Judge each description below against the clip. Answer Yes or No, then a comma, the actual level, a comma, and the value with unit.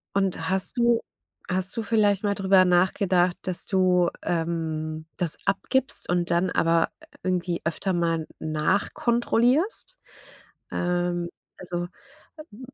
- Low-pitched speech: No, medium, 180 Hz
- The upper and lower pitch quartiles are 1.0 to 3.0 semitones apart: Yes, narrow, 2.6 semitones